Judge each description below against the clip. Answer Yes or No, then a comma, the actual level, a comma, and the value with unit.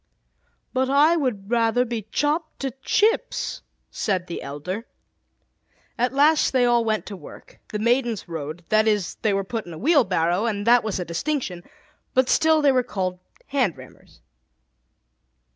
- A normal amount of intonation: No, wide, 5.9 semitones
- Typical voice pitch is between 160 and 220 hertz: No, high, 230 Hz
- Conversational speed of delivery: Yes, average, 160 wpm